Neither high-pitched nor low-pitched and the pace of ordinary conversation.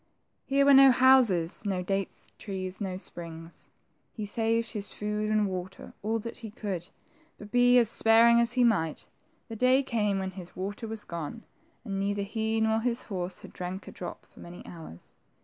No: high, 210 Hz; average, 185 wpm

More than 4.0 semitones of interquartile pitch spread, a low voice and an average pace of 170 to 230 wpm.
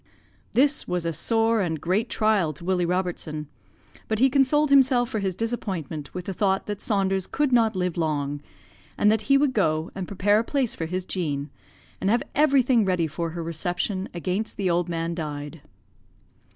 No: average, 5.0 semitones; high, 190 Hz; average, 180 wpm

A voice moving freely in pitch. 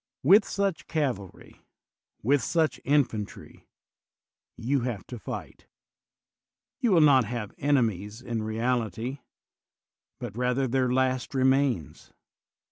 No: average, 3.7 semitones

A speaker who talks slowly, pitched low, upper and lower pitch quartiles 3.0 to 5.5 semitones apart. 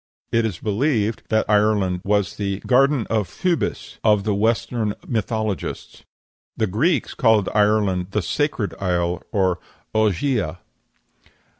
No: slow, 120 wpm; low, 105 Hz; narrow, 2.5 semitones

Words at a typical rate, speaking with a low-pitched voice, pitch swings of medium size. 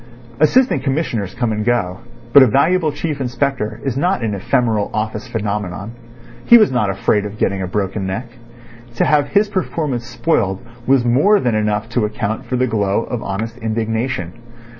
Yes: average, 170 wpm; low, 115 Hz; average, 4.6 semitones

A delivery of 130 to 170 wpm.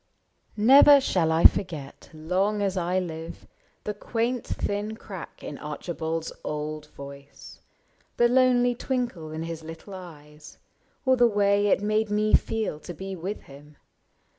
Yes: average, 140 wpm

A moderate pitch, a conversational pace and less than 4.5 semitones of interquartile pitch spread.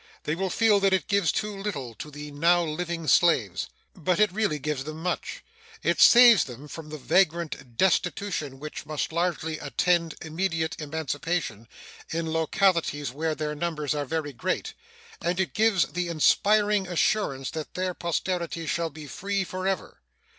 Yes: medium, 165 Hz; average, 155 wpm; average, 3.6 semitones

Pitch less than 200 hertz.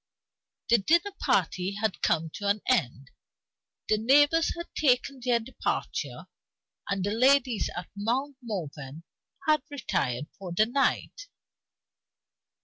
No: high, 225 Hz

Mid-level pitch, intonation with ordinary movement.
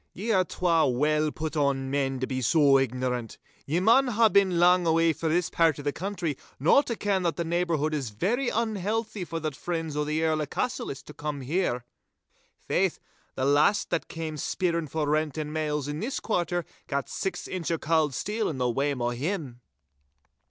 Yes: medium, 160 Hz; average, 4.2 semitones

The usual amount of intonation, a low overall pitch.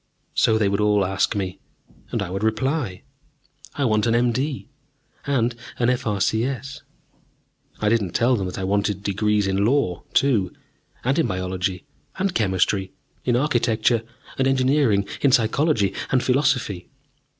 Yes: average, 4.7 semitones; low, 110 Hz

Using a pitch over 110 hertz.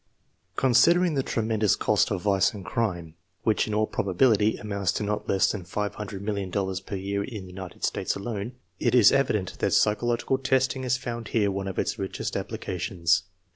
No: low, 105 Hz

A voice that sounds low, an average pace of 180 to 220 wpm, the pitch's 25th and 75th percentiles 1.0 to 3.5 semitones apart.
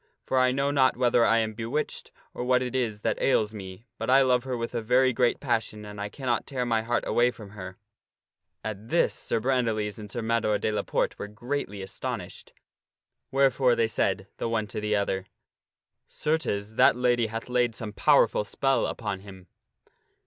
Yes: low, 115 Hz; average, 190 wpm; average, 3.2 semitones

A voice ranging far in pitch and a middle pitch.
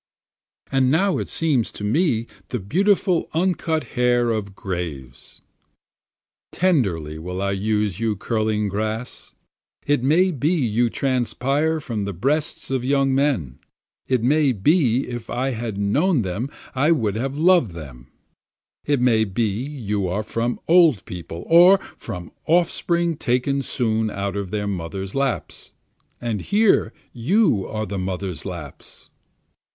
No: wide, 6.5 semitones; low, 120 Hz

